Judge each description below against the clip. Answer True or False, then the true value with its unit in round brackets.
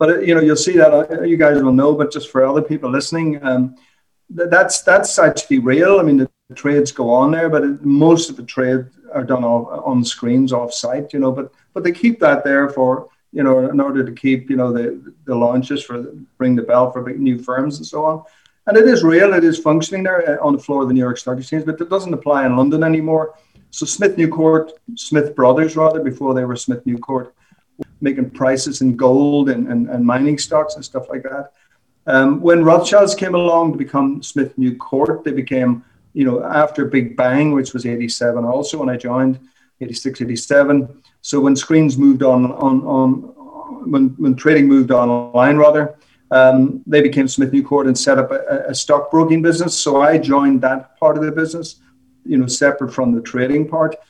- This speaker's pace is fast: True (215 wpm)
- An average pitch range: True (3.3 semitones)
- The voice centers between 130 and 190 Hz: True (140 Hz)